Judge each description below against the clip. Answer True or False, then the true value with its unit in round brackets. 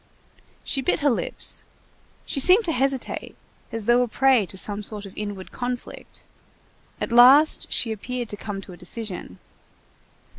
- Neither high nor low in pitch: False (235 Hz)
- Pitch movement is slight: False (4.4 semitones)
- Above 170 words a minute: False (155 wpm)